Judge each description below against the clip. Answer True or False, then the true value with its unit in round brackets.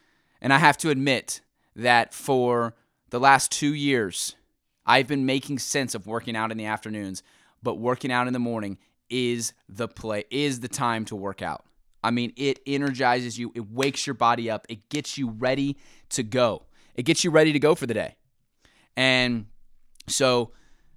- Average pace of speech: True (180 wpm)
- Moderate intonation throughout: True (3.2 semitones)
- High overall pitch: False (125 Hz)